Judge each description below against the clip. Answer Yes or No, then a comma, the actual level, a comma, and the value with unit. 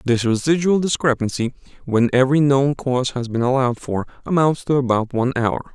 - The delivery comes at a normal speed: Yes, average, 165 wpm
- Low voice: Yes, low, 130 Hz